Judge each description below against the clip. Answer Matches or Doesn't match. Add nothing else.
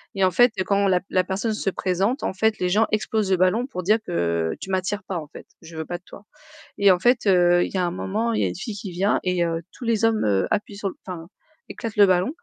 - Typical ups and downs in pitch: Matches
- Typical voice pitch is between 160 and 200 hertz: Matches